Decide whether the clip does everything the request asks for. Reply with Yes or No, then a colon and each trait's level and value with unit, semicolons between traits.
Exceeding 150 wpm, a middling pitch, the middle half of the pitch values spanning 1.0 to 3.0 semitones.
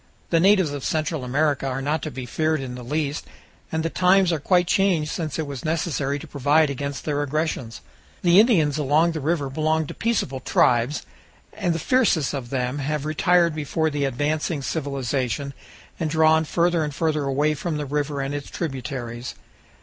Yes: average, 180 wpm; medium, 150 Hz; average, 2.7 semitones